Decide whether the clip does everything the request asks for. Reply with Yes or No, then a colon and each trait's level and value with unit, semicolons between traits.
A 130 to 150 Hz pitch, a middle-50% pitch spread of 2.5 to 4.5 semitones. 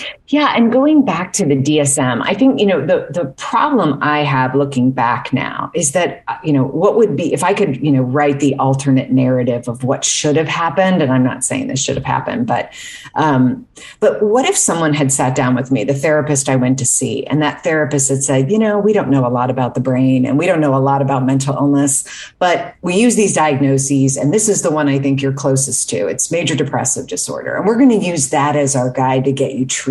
Yes: medium, 140 Hz; average, 4.1 semitones